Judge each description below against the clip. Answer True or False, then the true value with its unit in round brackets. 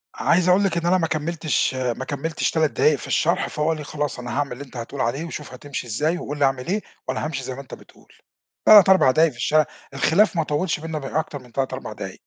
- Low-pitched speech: False (150 Hz)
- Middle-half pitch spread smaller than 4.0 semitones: True (3.6 semitones)